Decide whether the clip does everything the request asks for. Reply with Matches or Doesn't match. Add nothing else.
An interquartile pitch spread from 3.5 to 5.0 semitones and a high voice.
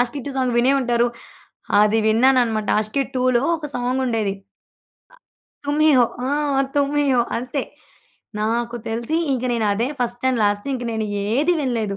Doesn't match